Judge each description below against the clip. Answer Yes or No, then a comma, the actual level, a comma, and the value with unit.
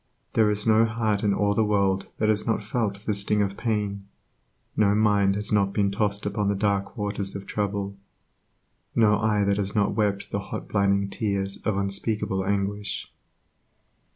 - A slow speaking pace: No, average, 175 wpm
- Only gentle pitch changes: Yes, narrow, 1.1 semitones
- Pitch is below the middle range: Yes, low, 100 Hz